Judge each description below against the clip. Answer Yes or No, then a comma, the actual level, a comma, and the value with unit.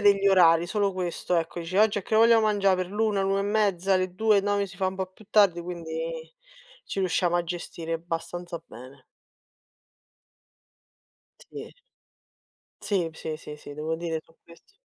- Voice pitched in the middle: Yes, medium, 180 Hz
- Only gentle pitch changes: No, average, 3.2 semitones